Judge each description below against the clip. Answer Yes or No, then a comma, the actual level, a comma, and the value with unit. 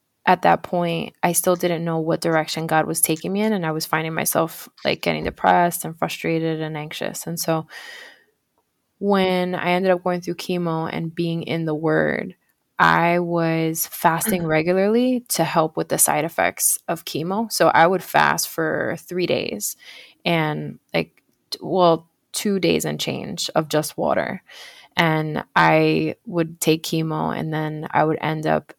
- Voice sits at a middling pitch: Yes, medium, 165 Hz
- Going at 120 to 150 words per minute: No, average, 165 wpm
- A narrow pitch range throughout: Yes, narrow, 2.3 semitones